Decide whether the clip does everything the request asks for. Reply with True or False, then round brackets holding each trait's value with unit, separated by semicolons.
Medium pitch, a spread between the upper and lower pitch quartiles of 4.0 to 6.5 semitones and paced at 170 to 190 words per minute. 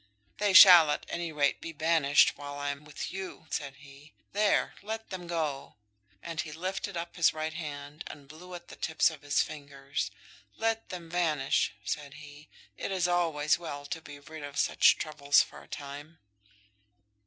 False (155 Hz; 3.3 semitones; 175 wpm)